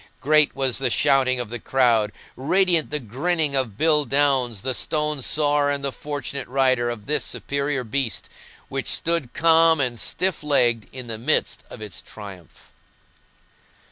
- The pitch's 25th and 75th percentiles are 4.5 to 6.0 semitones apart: No, average, 3.8 semitones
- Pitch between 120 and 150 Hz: Yes, low, 135 Hz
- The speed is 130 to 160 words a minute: Yes, average, 155 wpm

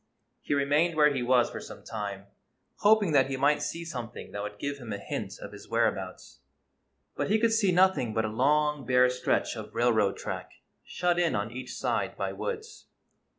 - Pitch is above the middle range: No, medium, 140 Hz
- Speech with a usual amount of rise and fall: No, wide, 6.8 semitones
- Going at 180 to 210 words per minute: Yes, average, 195 wpm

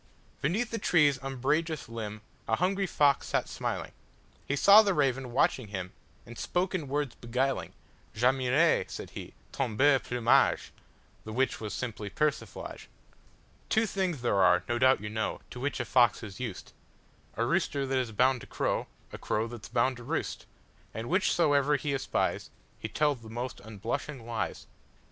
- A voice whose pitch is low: Yes, low, 130 Hz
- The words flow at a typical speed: Yes, average, 145 wpm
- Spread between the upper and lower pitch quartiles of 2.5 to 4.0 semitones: No, average, 4.4 semitones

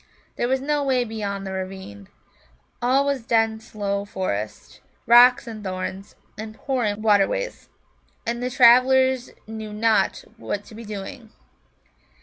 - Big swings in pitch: No, average, 3.8 semitones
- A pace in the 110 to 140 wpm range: Yes, slow, 135 wpm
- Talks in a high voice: Yes, high, 220 Hz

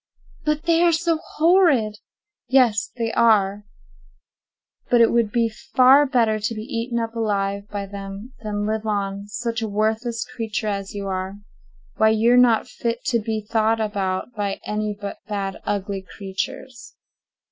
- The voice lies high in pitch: Yes, high, 220 Hz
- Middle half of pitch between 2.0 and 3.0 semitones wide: Yes, narrow, 2.6 semitones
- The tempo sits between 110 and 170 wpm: Yes, average, 150 wpm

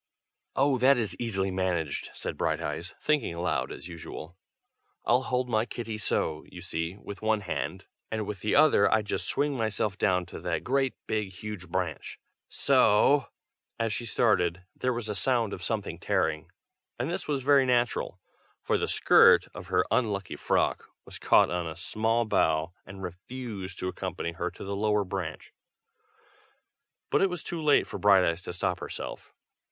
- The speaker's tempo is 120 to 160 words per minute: No, average, 170 wpm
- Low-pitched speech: Yes, low, 105 Hz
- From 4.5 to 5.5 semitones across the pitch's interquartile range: Yes, average, 5.1 semitones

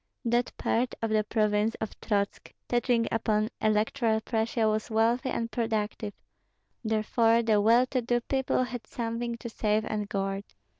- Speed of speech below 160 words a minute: Yes, average, 150 wpm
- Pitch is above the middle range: Yes, high, 225 Hz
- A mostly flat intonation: Yes, narrow, 1.7 semitones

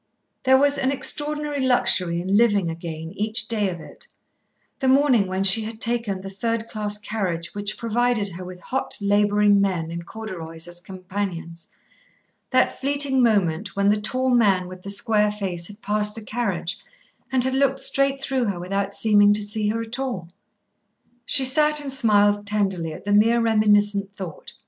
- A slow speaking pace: No, average, 170 wpm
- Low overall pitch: No, high, 210 Hz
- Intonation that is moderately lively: Yes, average, 3.9 semitones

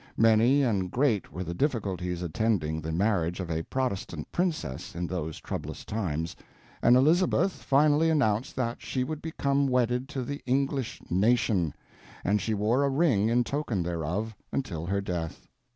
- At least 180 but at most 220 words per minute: No, average, 155 wpm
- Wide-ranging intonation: Yes, wide, 7.2 semitones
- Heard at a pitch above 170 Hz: No, low, 110 Hz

